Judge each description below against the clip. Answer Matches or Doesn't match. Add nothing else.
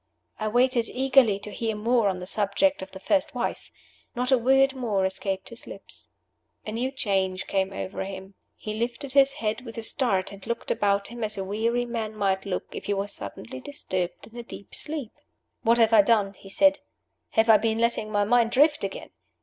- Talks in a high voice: Matches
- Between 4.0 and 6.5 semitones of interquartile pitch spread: Doesn't match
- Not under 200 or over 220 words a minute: Matches